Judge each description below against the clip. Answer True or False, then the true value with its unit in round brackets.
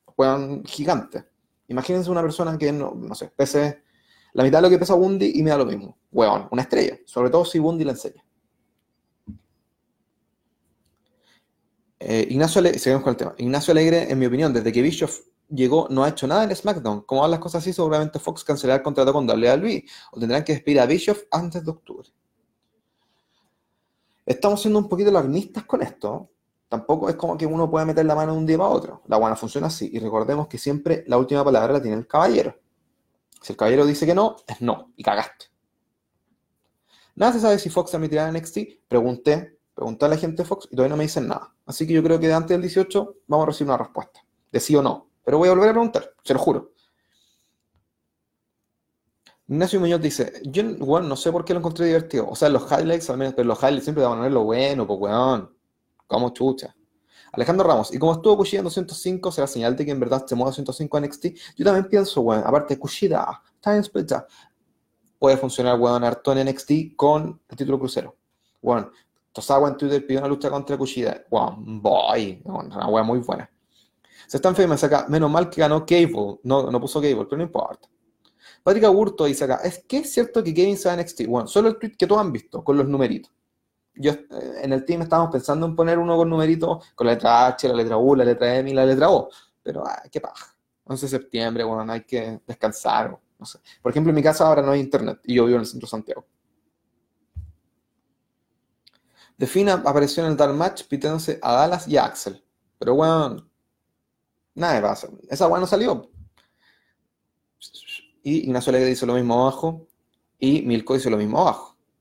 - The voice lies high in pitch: False (150 Hz)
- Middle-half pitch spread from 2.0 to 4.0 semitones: False (4.4 semitones)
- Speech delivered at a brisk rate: True (205 wpm)